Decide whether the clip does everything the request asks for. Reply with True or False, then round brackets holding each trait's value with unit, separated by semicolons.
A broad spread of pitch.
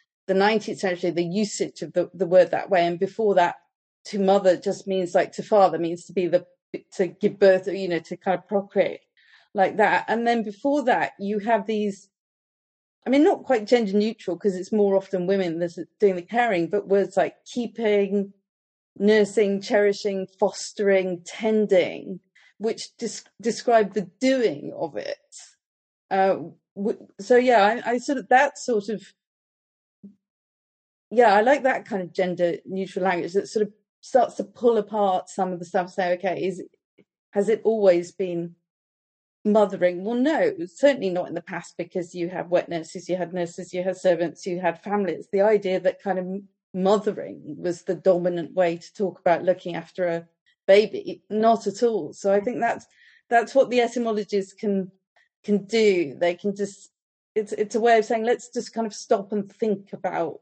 False (3.3 semitones)